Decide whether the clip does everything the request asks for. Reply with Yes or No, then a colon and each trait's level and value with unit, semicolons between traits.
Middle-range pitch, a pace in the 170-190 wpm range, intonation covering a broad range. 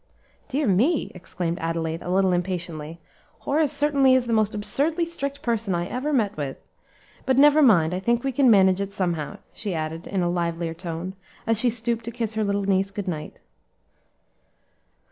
No: high, 200 Hz; average, 180 wpm; wide, 6.4 semitones